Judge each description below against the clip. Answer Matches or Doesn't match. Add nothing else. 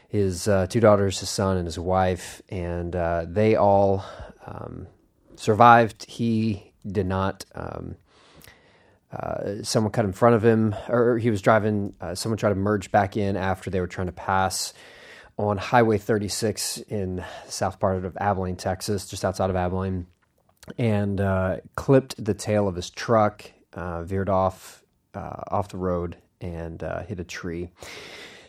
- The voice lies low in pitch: Matches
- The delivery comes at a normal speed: Matches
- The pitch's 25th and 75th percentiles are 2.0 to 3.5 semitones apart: Matches